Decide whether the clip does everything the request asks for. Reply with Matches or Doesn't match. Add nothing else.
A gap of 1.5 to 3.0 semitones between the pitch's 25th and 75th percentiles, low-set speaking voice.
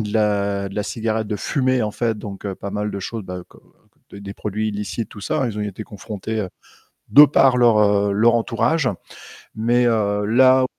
Matches